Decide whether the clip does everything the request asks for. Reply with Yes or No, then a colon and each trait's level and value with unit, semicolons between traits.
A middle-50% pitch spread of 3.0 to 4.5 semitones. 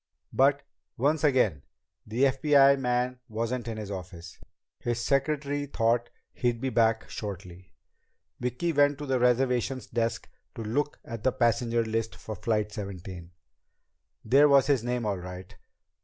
Yes: average, 3.8 semitones